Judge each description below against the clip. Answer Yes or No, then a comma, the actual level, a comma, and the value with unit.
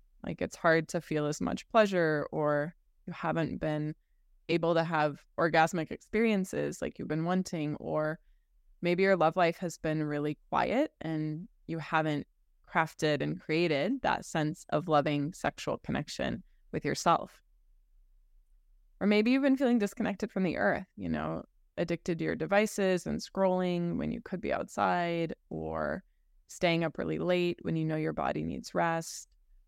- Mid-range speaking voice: Yes, medium, 165 Hz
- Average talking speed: Yes, average, 160 wpm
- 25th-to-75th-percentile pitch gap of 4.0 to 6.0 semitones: No, average, 3.3 semitones